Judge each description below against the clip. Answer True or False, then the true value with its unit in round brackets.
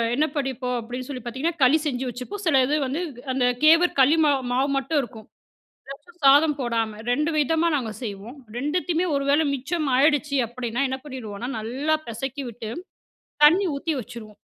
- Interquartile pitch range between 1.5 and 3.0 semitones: False (3.6 semitones)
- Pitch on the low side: False (270 Hz)